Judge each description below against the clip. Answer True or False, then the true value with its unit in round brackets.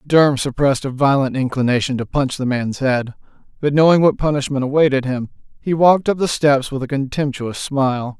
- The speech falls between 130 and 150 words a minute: False (185 wpm)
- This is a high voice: False (135 Hz)